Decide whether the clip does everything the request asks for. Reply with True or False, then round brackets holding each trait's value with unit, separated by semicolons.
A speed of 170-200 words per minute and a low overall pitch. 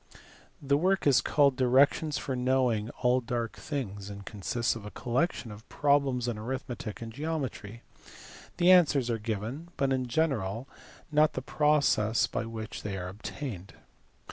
False (150 wpm; 125 Hz)